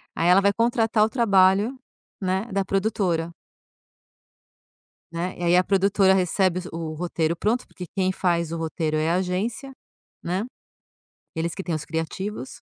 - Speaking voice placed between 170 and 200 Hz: Yes, medium, 185 Hz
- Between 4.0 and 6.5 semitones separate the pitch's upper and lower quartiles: No, average, 3.0 semitones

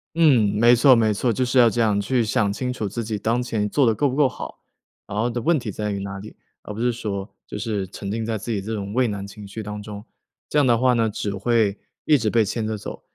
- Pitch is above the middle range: No, low, 110 Hz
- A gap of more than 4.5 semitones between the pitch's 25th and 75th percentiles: No, average, 2.9 semitones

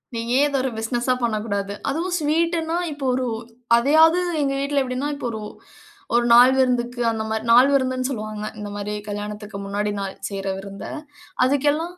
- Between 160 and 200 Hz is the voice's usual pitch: No, high, 245 Hz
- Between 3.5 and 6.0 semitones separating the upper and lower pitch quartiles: Yes, average, 5.0 semitones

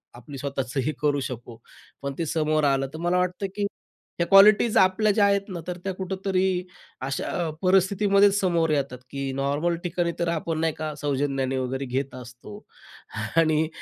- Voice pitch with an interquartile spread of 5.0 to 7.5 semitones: Yes, average, 5.3 semitones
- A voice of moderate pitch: Yes, medium, 155 Hz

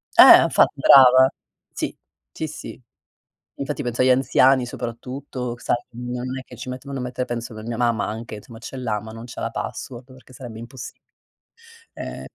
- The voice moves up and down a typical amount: No, narrow, 1.8 semitones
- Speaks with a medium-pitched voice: No, low, 125 Hz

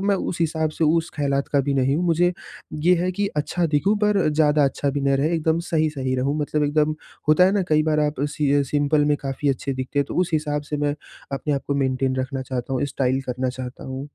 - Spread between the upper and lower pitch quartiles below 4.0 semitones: Yes, narrow, 2.5 semitones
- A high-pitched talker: No, medium, 145 Hz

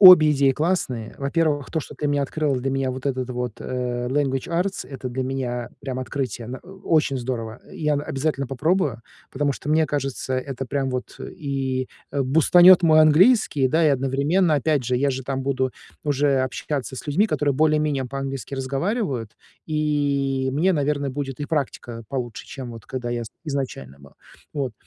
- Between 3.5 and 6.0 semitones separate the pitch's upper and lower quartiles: No, narrow, 2.6 semitones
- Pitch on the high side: No, low, 135 Hz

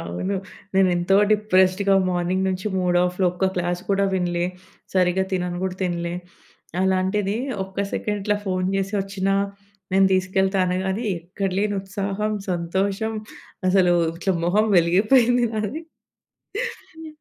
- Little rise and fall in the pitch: Yes, narrow, 1.8 semitones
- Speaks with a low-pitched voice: No, high, 190 Hz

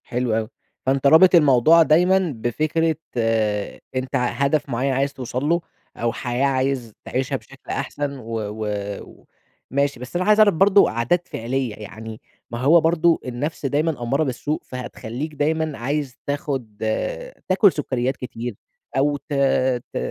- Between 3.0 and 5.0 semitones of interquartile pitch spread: Yes, average, 4.3 semitones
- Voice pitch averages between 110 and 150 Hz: Yes, low, 135 Hz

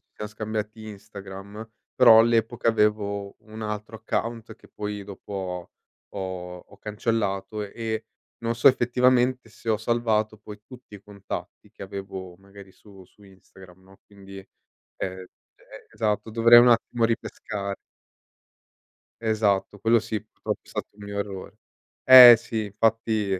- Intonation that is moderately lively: No, narrow, 2.3 semitones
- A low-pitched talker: Yes, low, 105 Hz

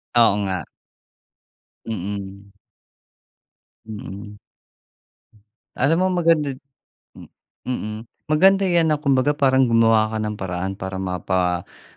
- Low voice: Yes, low, 110 Hz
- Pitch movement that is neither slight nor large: No, wide, 6.1 semitones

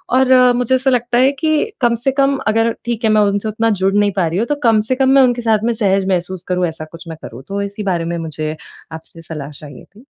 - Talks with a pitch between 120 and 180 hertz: No, high, 210 Hz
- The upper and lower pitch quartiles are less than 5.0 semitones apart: No, wide, 5.6 semitones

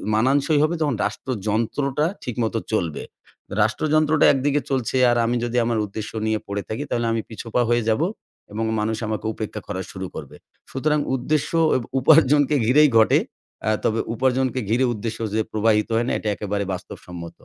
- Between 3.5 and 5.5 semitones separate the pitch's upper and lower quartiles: Yes, average, 4.0 semitones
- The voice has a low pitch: Yes, low, 115 Hz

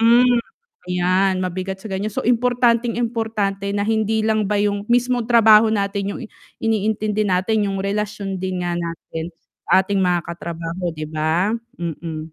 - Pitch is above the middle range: Yes, high, 200 Hz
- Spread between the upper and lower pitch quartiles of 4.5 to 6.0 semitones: No, average, 3.4 semitones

